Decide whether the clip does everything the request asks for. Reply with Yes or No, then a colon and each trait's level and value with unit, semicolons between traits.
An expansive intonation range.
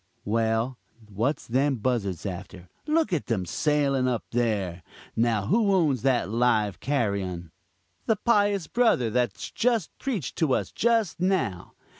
Yes: wide, 8.7 semitones